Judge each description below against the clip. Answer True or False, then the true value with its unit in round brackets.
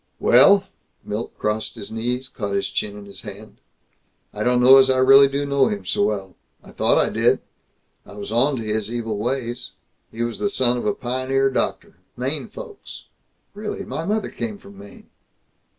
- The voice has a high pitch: False (120 Hz)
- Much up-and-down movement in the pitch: False (4.2 semitones)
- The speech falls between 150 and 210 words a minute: True (180 wpm)